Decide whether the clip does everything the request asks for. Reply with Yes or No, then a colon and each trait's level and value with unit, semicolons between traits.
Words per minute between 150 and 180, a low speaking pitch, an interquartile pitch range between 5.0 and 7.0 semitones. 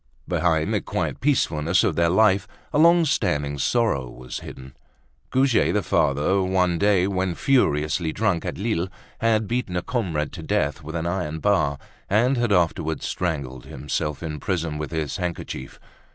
Yes: average, 160 wpm; very low, 85 Hz; wide, 5.5 semitones